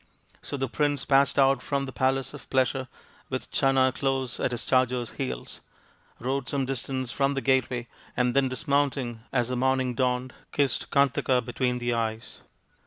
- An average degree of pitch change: No, narrow, 1.6 semitones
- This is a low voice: Yes, low, 130 Hz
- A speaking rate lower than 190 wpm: Yes, average, 170 wpm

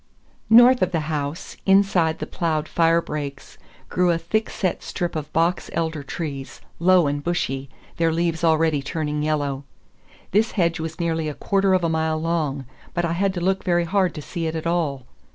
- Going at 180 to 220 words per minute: Yes, average, 190 wpm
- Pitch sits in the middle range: Yes, medium, 165 Hz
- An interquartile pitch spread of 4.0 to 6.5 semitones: No, narrow, 2.4 semitones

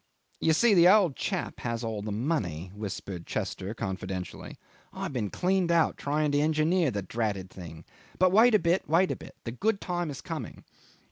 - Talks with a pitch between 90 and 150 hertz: Yes, medium, 140 Hz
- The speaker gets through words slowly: No, average, 185 wpm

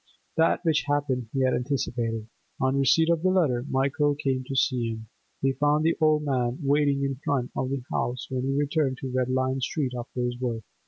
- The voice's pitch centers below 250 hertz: Yes, low, 135 Hz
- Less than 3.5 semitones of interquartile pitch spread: Yes, narrow, 2.5 semitones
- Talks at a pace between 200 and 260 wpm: Yes, fast, 205 wpm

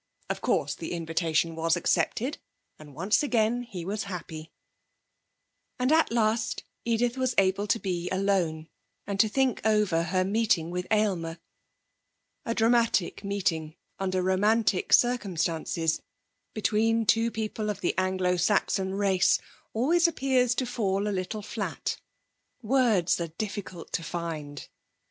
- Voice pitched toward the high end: Yes, high, 195 Hz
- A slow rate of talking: Yes, slow, 130 wpm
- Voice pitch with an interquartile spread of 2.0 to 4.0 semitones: No, average, 4.7 semitones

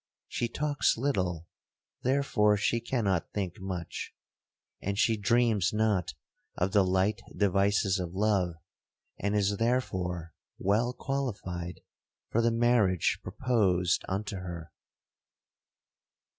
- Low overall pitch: Yes, low, 100 Hz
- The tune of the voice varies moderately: Yes, average, 4.0 semitones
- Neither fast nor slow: No, slow, 105 wpm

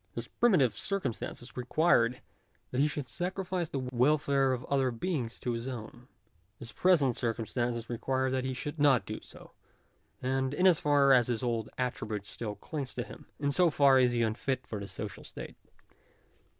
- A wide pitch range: No, average, 3.3 semitones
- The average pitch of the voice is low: Yes, low, 130 Hz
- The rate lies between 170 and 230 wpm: Yes, average, 175 wpm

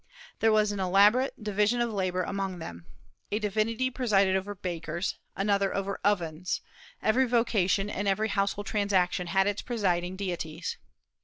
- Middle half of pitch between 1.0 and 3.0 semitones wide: Yes, narrow, 2.4 semitones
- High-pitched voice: Yes, high, 200 Hz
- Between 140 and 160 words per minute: Yes, average, 145 wpm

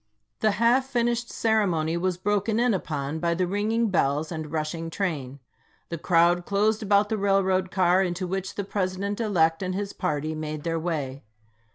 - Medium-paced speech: Yes, average, 175 wpm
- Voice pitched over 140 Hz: Yes, medium, 185 Hz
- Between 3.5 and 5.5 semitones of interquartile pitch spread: Yes, average, 4.1 semitones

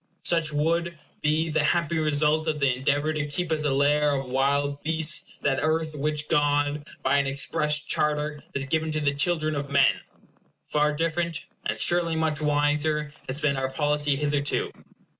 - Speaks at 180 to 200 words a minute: No, average, 170 wpm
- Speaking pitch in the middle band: Yes, medium, 150 Hz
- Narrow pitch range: Yes, narrow, 1.7 semitones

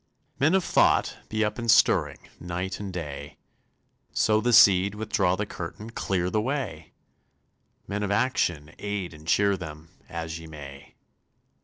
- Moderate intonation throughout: Yes, average, 4.5 semitones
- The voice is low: Yes, very low, 95 Hz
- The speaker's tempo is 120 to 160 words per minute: Yes, average, 150 wpm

